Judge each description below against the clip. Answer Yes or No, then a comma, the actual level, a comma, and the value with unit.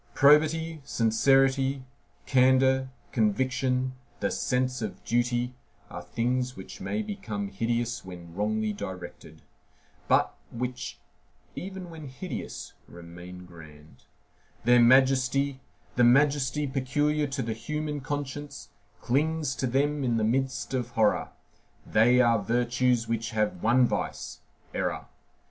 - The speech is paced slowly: Yes, slow, 115 wpm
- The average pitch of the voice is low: Yes, low, 125 Hz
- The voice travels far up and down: No, average, 3.4 semitones